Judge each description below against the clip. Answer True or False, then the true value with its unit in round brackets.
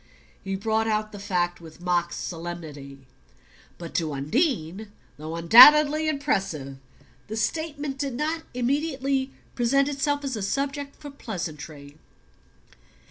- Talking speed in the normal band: False (120 wpm)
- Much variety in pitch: True (8.8 semitones)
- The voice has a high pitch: True (220 Hz)